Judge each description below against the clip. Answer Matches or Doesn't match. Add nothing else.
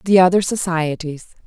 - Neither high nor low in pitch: Matches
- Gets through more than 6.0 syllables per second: Doesn't match